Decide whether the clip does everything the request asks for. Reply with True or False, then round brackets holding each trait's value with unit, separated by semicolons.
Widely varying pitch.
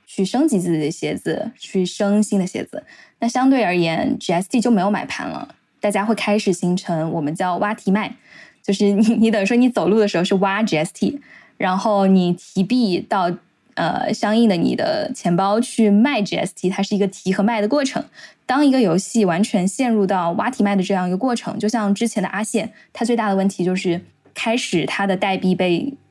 False (3.6 semitones)